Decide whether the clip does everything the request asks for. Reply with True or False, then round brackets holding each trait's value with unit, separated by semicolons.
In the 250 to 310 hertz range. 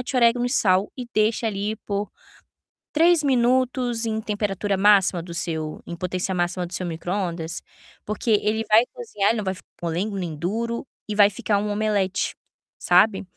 False (205 Hz)